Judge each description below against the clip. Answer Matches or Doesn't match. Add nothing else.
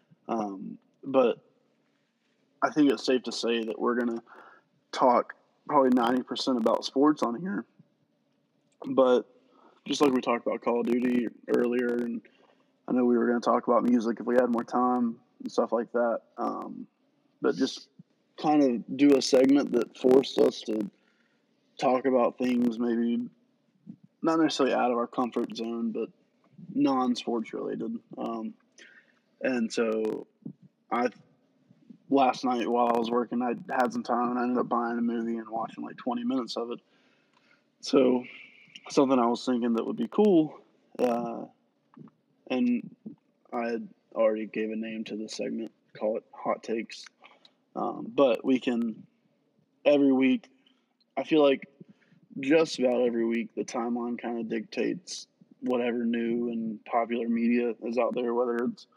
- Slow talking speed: Doesn't match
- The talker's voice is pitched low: Matches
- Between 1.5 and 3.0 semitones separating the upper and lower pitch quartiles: Doesn't match